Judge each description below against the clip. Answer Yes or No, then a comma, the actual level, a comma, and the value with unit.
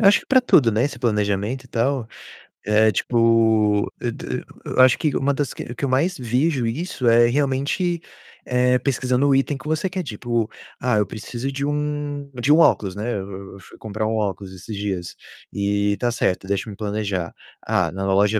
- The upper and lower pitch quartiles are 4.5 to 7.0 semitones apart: Yes, average, 4.9 semitones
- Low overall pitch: Yes, low, 120 Hz